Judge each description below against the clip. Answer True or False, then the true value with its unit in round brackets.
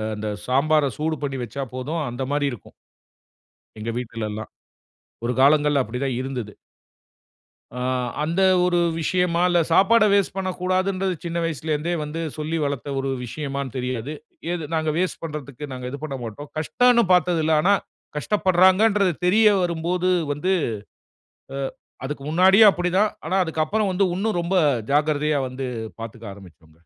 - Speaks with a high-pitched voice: False (155 Hz)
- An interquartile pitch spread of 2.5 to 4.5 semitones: False (5.2 semitones)